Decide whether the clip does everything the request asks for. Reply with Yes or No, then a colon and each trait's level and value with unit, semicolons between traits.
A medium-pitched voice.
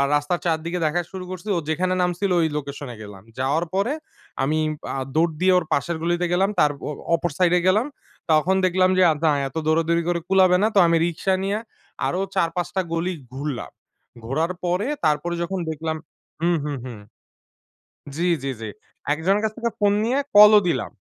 Yes: medium, 170 Hz